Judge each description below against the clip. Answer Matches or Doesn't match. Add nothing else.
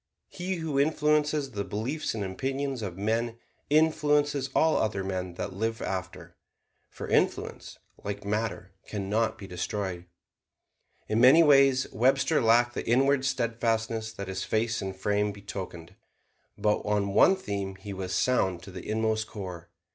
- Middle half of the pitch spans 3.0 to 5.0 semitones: Doesn't match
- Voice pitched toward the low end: Matches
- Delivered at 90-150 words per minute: Matches